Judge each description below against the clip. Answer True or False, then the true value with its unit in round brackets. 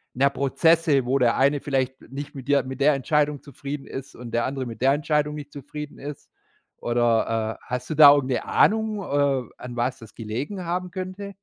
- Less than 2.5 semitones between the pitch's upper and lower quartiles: False (2.9 semitones)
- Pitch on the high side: False (140 Hz)